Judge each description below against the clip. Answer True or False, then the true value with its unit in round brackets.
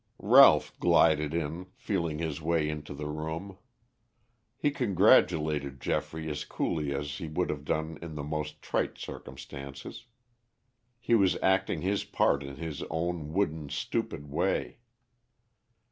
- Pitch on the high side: False (80 Hz)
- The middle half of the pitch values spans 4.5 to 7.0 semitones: False (2.9 semitones)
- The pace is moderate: False (130 wpm)